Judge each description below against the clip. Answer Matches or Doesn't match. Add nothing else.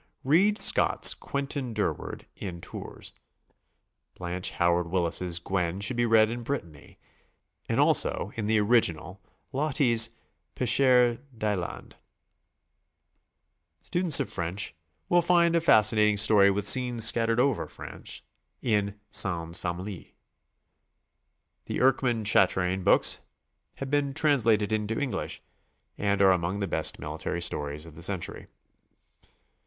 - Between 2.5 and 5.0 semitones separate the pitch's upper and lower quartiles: Doesn't match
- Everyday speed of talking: Doesn't match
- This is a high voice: Doesn't match